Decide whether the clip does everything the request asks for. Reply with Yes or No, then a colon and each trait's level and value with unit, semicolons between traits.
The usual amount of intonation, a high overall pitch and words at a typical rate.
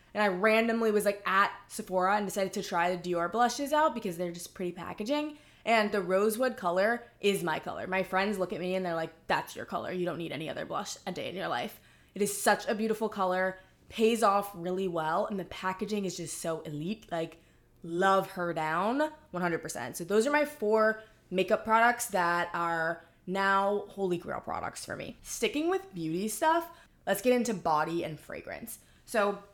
Yes: average, 3.9 semitones; high, 195 Hz; average, 195 wpm